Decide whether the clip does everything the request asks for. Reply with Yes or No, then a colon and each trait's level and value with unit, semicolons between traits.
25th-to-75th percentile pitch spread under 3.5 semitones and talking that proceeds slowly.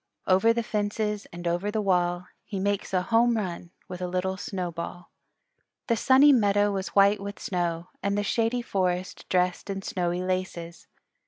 No: narrow, 2.6 semitones; average, 165 wpm